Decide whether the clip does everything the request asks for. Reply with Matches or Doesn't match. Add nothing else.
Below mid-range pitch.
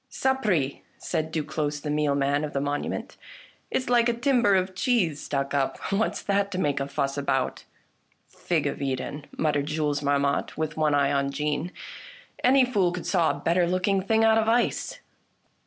Doesn't match